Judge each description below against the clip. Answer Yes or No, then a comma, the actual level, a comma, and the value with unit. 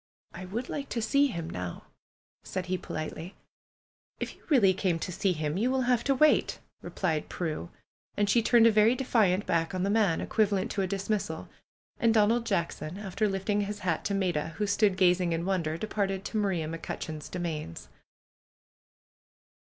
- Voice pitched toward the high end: Yes, high, 195 Hz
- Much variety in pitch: No, average, 4.1 semitones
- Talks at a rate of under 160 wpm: No, average, 175 wpm